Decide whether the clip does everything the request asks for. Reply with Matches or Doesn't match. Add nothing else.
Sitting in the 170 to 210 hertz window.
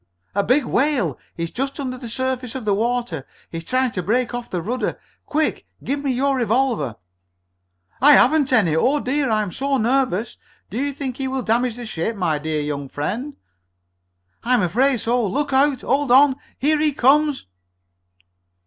Doesn't match